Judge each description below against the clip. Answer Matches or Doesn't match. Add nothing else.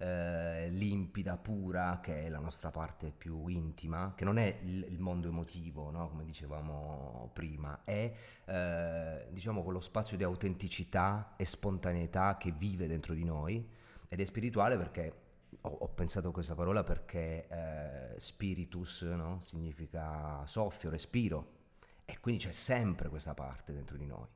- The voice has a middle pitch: Doesn't match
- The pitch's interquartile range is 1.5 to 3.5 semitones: Matches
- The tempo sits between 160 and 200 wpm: Doesn't match